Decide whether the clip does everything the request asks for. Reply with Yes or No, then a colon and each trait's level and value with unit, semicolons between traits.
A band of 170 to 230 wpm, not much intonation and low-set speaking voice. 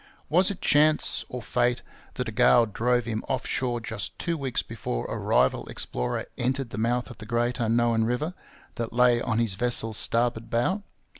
Yes: average, 180 wpm; narrow, 1.6 semitones; low, 120 Hz